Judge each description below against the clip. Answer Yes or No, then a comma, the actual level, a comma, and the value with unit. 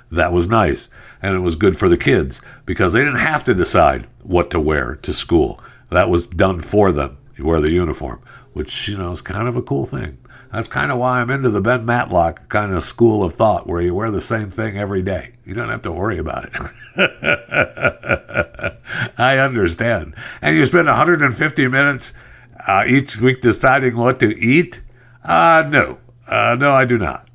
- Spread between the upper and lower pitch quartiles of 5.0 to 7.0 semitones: Yes, wide, 5.5 semitones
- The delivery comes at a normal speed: Yes, average, 195 wpm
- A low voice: Yes, low, 115 Hz